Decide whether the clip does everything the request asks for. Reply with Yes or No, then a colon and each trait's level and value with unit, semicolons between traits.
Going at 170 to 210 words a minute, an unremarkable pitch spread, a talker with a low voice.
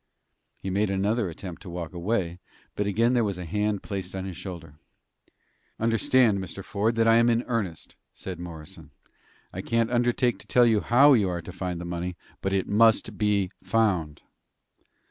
Yes: average, 180 wpm; average, 4.1 semitones; low, 100 Hz